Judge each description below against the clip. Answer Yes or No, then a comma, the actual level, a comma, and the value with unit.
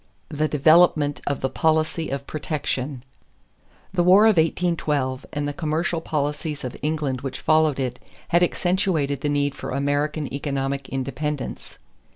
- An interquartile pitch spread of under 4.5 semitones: Yes, narrow, 2.4 semitones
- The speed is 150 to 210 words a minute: No, average, 140 wpm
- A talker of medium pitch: Yes, medium, 150 Hz